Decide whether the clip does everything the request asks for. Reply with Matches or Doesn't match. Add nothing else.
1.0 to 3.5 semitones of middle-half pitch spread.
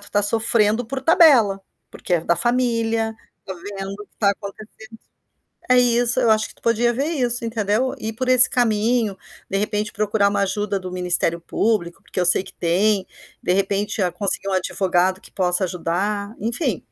Matches